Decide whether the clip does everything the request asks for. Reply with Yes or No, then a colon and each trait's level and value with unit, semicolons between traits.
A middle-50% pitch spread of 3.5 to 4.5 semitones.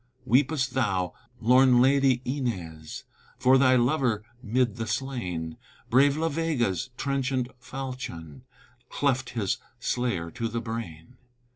Yes: average, 4.0 semitones